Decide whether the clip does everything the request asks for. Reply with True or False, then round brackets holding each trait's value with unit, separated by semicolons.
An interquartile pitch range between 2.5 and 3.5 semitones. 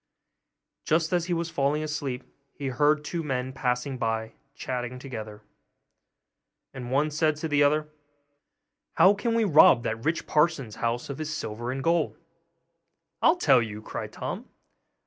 False (4.2 semitones)